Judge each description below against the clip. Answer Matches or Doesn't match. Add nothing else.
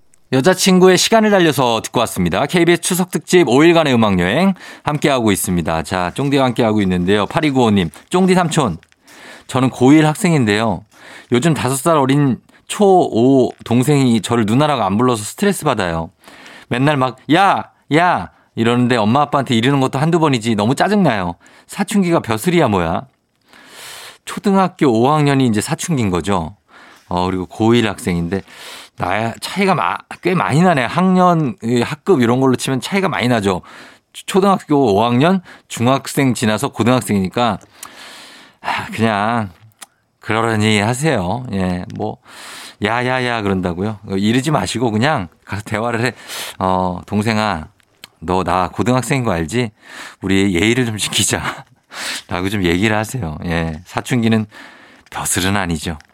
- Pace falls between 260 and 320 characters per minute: Matches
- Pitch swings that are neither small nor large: Doesn't match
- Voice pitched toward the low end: Matches